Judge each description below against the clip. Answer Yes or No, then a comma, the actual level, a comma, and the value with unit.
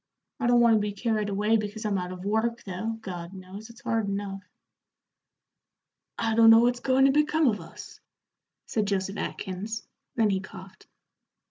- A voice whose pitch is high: Yes, high, 215 Hz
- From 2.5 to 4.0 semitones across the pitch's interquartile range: Yes, average, 2.8 semitones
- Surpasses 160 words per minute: Yes, average, 170 wpm